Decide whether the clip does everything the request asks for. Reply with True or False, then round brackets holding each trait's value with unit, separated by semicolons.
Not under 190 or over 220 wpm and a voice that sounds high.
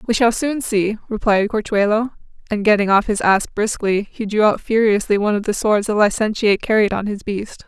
True (205 wpm; 210 Hz)